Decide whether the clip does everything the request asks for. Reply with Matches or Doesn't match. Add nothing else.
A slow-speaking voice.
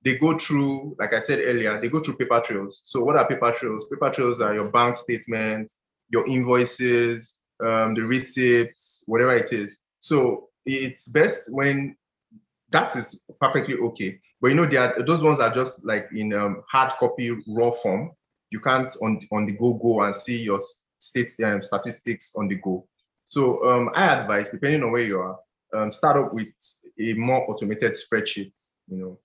Doesn't match